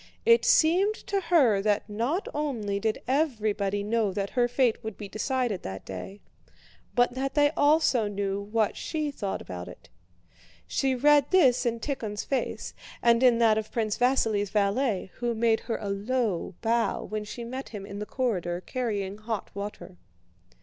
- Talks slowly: No, average, 165 wpm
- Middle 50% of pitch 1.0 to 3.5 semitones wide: No, average, 4.3 semitones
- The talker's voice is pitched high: Yes, high, 225 Hz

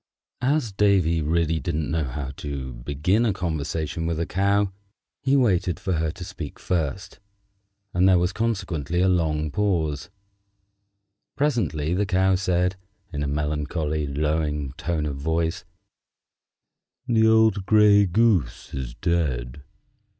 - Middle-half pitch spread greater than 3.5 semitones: Yes, average, 4.5 semitones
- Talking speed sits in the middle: No, slow, 130 wpm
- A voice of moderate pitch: No, very low, 85 Hz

